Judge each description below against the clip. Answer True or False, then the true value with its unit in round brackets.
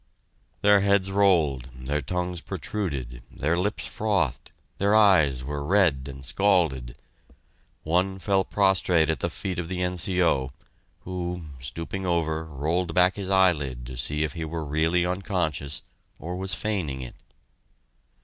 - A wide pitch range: False (4.7 semitones)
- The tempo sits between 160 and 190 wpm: False (140 wpm)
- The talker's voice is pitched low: True (85 Hz)